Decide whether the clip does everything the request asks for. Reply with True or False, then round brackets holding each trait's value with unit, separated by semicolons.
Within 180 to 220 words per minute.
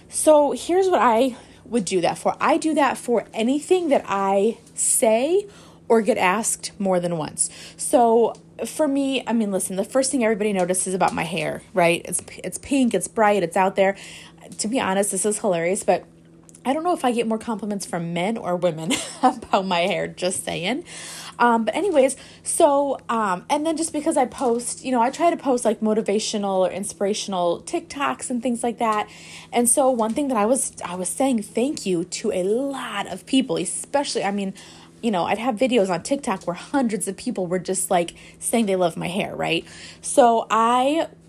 True (200 wpm)